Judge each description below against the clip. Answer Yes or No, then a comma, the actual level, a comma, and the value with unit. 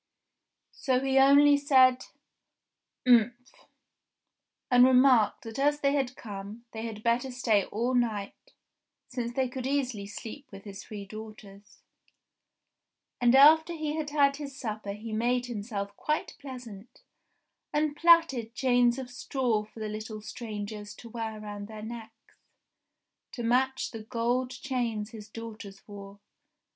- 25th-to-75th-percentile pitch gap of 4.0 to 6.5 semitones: No, average, 3.6 semitones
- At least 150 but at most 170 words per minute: No, slow, 135 wpm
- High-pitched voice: Yes, high, 240 Hz